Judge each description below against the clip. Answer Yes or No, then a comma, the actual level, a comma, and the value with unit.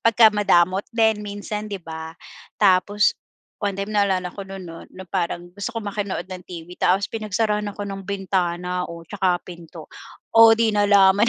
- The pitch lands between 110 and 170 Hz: No, high, 195 Hz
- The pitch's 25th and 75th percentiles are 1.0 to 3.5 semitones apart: Yes, narrow, 2.6 semitones